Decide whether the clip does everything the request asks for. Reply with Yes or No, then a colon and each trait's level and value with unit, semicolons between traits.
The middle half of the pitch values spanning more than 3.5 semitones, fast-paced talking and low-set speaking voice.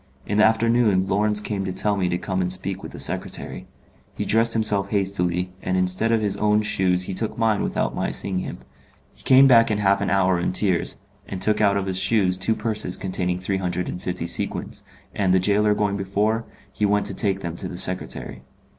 No: narrow, 2.5 semitones; fast, 215 wpm; low, 100 Hz